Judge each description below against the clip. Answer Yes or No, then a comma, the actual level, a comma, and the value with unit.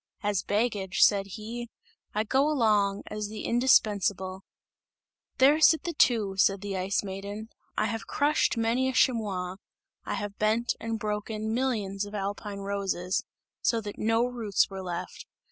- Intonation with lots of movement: No, average, 2.8 semitones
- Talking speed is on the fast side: No, average, 150 wpm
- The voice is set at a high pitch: Yes, high, 210 Hz